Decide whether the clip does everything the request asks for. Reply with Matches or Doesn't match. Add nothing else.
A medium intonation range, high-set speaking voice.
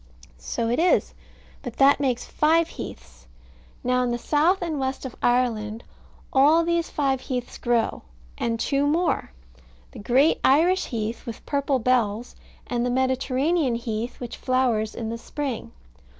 Matches